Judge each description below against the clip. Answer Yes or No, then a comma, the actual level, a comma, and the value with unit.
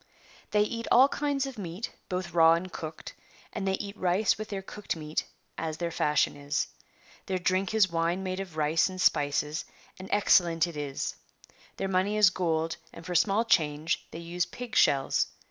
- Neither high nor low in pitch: Yes, medium, 180 Hz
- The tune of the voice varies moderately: Yes, average, 3.6 semitones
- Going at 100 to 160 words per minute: No, average, 180 wpm